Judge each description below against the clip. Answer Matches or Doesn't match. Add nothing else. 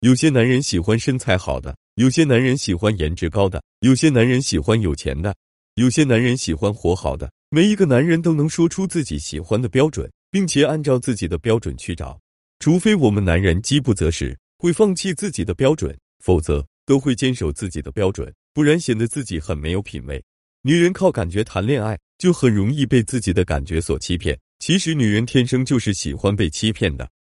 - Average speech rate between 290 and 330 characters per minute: Matches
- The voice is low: Matches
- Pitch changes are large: Matches